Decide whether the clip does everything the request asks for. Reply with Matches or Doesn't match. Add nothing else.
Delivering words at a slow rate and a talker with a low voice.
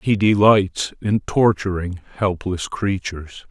Matches